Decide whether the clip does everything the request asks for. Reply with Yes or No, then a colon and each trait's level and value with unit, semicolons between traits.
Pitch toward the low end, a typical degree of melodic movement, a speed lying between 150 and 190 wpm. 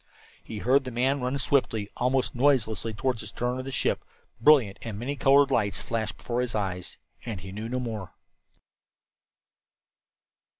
Yes: low, 120 Hz; average, 3.5 semitones; average, 160 wpm